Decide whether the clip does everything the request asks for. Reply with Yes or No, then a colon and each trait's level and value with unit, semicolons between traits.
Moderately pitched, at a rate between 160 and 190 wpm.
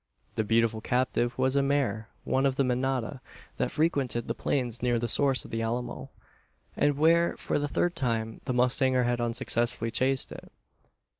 No: low, 125 Hz; average, 170 wpm